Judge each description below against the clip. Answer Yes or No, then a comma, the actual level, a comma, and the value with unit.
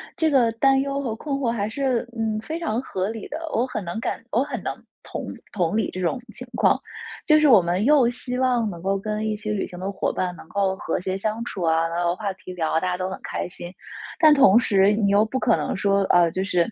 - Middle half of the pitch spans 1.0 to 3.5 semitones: No, average, 5.0 semitones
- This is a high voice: Yes, high, 215 Hz